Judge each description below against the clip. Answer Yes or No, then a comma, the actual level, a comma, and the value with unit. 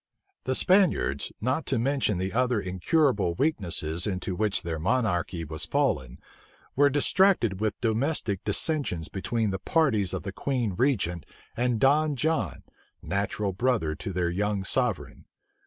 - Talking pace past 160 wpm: No, average, 140 wpm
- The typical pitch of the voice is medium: No, low, 105 Hz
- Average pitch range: No, wide, 6.4 semitones